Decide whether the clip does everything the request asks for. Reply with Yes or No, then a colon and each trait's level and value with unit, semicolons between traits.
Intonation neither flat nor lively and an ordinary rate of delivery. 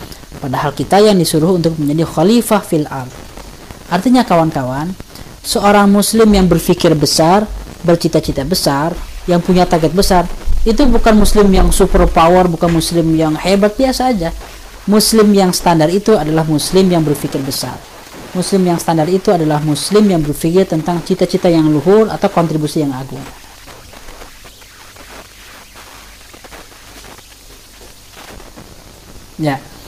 Yes: average, 4.5 semitones; average, 120 wpm